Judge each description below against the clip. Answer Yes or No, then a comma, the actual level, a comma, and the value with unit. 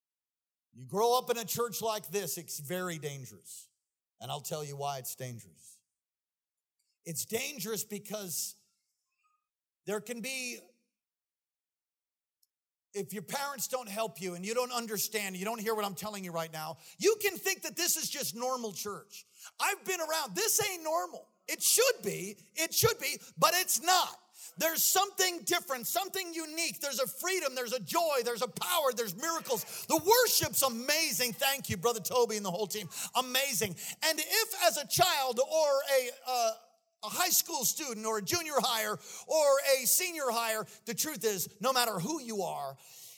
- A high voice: Yes, high, 245 Hz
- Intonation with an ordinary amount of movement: No, wide, 7.8 semitones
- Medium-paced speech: Yes, average, 170 wpm